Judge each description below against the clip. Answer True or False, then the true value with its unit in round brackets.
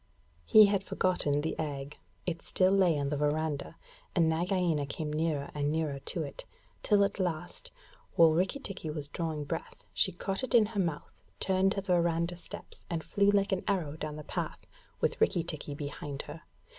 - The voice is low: False (165 Hz)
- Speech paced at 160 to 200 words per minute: True (185 wpm)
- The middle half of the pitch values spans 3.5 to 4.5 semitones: True (4.0 semitones)